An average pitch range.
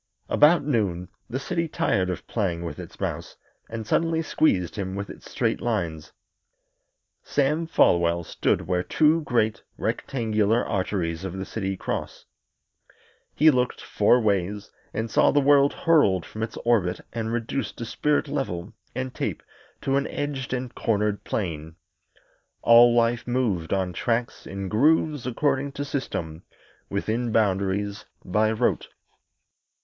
No: wide, 5.8 semitones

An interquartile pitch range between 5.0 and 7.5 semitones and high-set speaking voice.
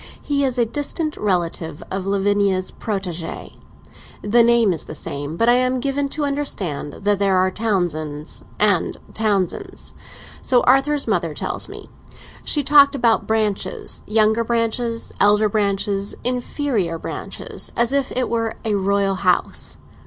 No: average, 4.4 semitones; high, 215 Hz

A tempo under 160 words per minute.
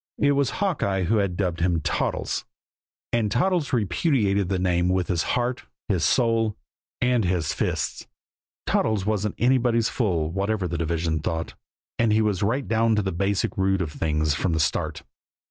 No: average, 165 wpm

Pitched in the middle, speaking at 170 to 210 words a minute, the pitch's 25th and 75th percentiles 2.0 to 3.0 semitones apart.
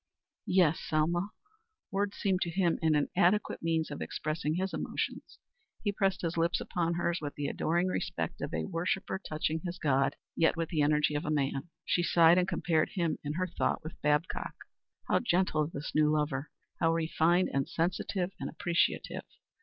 Yes: medium, 165 Hz; average, 175 wpm; average, 2.7 semitones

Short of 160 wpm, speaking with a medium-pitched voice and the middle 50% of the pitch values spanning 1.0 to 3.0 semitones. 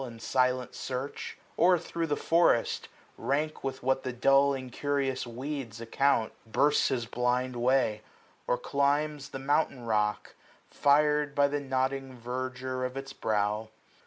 No: average, 140 wpm; low, 130 Hz; narrow, 2.5 semitones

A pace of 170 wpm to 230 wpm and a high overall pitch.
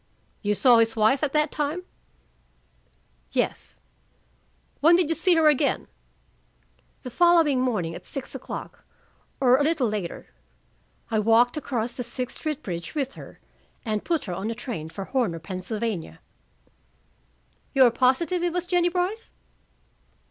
No: average, 145 wpm; very high, 255 Hz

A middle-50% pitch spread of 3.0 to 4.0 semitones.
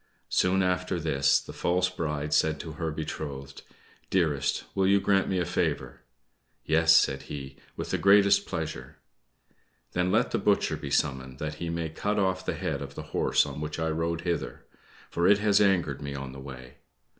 No: average, 4.4 semitones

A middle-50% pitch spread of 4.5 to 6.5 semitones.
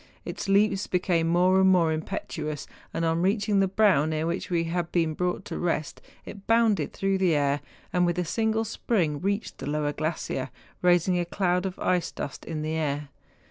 No: average, 3.5 semitones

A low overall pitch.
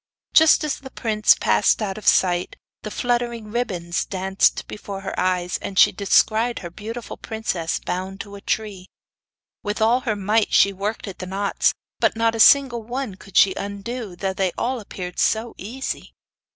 No: high, 210 Hz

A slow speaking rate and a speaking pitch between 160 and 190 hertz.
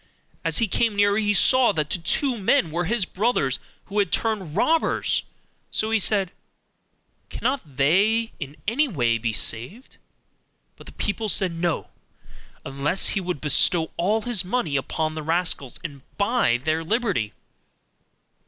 No: average, 150 wpm; medium, 185 Hz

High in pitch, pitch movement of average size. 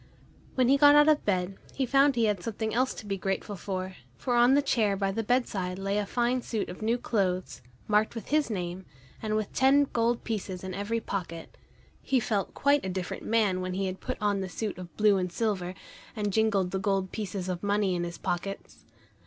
Yes: high, 205 Hz; average, 3.7 semitones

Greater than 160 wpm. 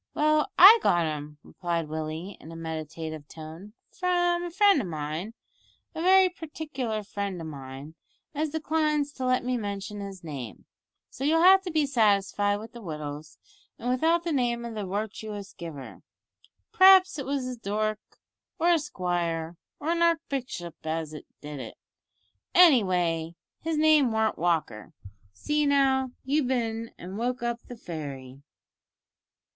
No: average, 150 wpm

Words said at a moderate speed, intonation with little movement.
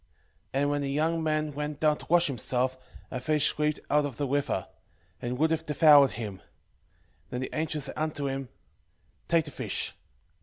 Yes: average, 190 wpm; narrow, 2.2 semitones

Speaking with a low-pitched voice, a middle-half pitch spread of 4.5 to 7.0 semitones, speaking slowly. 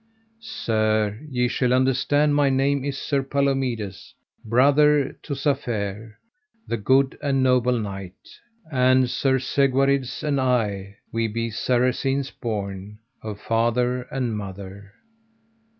No: low, 125 Hz; average, 3.8 semitones; slow, 115 wpm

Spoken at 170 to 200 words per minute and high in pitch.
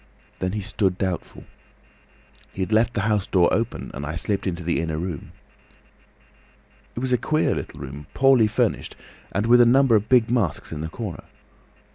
No: average, 180 wpm; low, 100 Hz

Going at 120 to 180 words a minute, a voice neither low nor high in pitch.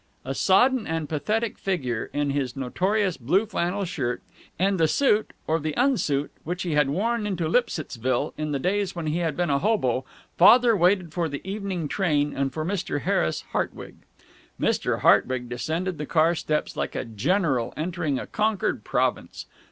Yes: average, 170 wpm; medium, 165 Hz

